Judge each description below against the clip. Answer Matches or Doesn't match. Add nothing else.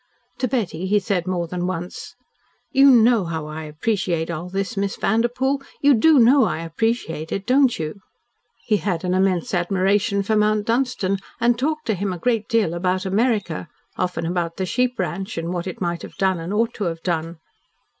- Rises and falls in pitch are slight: Doesn't match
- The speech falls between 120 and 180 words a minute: Doesn't match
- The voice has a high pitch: Matches